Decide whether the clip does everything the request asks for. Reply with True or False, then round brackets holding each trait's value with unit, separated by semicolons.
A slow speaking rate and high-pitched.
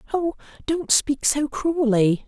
True (130 wpm; 280 Hz)